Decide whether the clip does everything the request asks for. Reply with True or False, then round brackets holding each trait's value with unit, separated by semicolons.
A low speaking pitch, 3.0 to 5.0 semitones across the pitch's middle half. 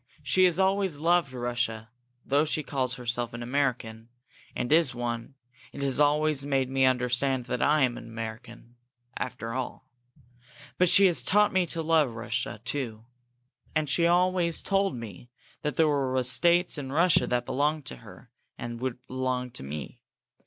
True (130 Hz; 4.4 semitones)